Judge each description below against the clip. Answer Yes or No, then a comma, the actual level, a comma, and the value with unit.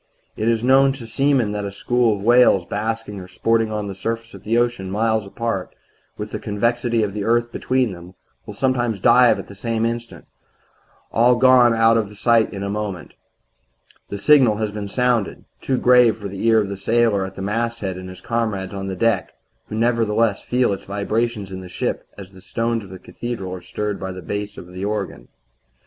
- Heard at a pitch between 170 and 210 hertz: No, low, 110 Hz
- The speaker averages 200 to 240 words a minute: Yes, fast, 205 wpm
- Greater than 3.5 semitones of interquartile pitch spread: No, average, 3.1 semitones